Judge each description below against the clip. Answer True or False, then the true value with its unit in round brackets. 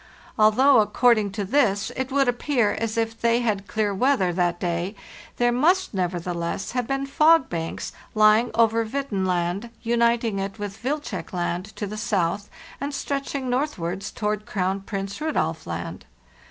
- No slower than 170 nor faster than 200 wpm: False (155 wpm)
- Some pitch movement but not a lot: True (4.5 semitones)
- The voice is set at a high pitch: True (215 Hz)